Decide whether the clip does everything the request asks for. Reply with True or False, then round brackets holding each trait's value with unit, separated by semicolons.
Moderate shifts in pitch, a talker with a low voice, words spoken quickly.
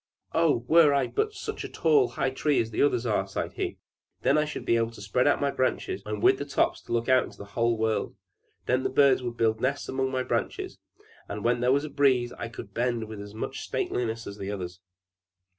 True (3.8 semitones; 120 Hz; 225 wpm)